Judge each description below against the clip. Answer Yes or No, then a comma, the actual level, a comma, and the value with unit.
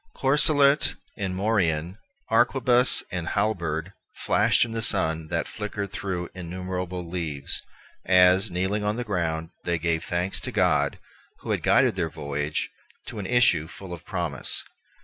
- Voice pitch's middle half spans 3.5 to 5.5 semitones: Yes, average, 3.9 semitones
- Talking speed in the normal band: Yes, average, 145 wpm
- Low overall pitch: Yes, very low, 90 Hz